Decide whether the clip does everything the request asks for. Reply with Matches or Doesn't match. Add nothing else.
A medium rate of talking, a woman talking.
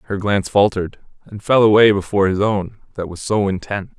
Doesn't match